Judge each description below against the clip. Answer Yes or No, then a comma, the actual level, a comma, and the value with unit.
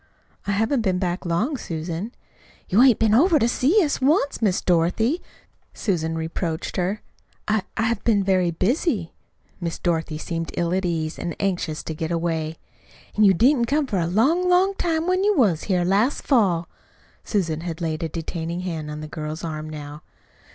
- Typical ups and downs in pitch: No, wide, 6.2 semitones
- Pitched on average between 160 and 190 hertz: Yes, medium, 185 Hz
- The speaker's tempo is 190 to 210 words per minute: No, average, 180 wpm